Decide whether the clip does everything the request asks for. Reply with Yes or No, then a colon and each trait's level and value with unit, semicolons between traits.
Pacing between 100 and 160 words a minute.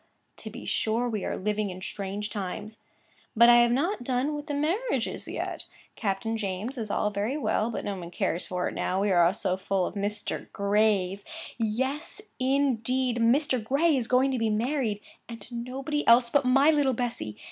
No: average, 190 wpm